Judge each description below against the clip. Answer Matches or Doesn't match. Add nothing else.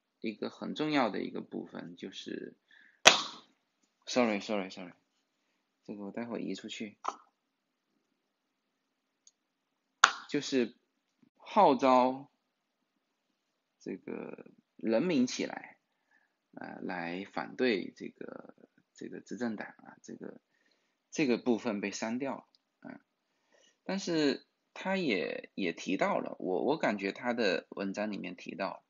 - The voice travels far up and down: Matches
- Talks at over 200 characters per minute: Doesn't match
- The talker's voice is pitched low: Matches